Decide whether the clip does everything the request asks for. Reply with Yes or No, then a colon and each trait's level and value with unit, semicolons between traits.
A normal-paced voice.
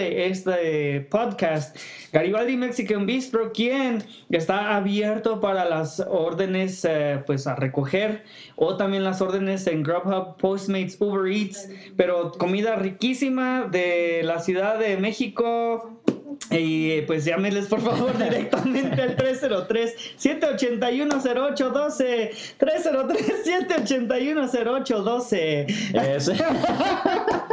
No: slow, 100 wpm